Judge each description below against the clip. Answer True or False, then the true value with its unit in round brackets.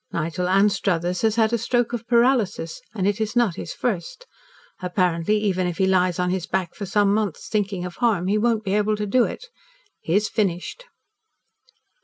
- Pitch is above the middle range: True (200 Hz)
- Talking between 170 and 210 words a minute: True (190 wpm)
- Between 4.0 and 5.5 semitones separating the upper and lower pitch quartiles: False (3.5 semitones)